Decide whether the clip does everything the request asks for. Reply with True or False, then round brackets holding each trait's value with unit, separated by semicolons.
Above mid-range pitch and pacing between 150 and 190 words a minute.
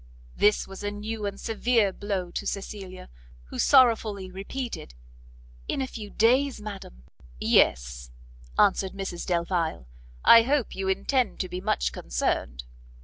False (200 Hz; 135 wpm)